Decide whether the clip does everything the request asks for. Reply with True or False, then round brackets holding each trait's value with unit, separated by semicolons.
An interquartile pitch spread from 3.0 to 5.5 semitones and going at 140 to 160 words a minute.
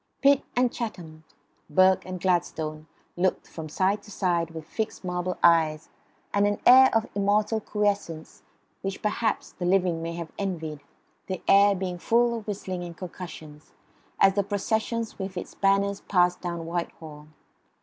True (3.4 semitones; 150 wpm)